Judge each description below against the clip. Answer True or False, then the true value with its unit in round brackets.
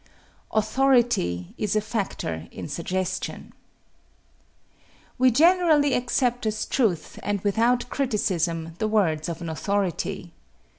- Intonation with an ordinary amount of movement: False (6.2 semitones)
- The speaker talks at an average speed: False (105 wpm)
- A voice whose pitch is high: True (210 Hz)